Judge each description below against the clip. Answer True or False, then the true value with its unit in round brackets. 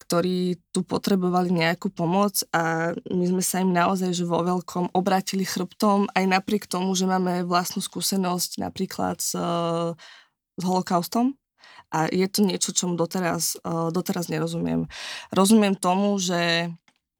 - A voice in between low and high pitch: True (180 Hz)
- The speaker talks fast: False (140 wpm)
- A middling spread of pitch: False (2.3 semitones)